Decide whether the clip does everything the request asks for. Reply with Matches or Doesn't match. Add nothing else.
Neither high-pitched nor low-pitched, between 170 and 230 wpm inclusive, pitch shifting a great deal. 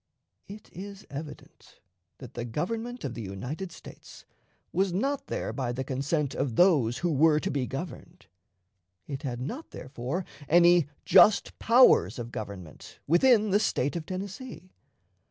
Doesn't match